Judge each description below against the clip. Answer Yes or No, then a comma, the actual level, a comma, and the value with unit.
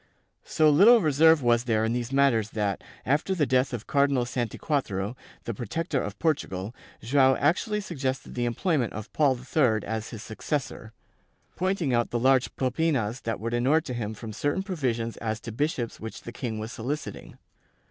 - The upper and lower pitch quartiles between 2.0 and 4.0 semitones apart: No, average, 4.5 semitones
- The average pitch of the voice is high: No, low, 125 Hz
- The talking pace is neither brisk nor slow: Yes, average, 170 wpm